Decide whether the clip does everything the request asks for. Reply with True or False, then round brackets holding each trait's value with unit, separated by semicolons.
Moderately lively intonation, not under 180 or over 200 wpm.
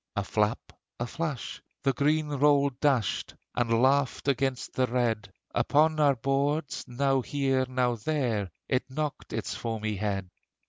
False (3.2 semitones; 140 wpm)